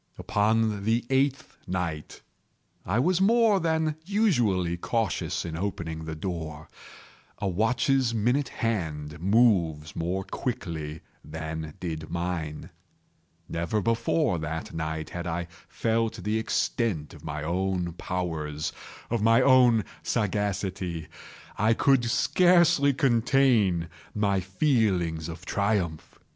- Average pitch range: No, wide, 6.2 semitones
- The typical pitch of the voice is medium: No, very low, 95 Hz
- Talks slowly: Yes, slow, 105 wpm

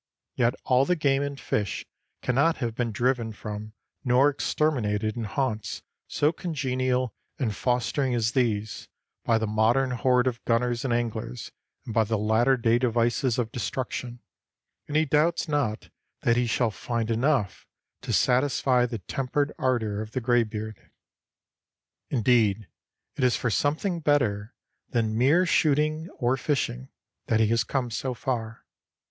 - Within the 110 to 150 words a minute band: Yes, average, 145 wpm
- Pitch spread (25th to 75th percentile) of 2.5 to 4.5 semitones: Yes, average, 3.3 semitones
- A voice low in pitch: Yes, low, 120 Hz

